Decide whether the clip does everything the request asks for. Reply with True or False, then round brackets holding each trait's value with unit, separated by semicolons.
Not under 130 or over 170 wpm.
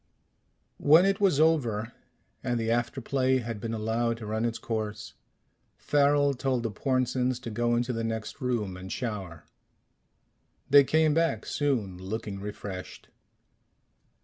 True (140 wpm)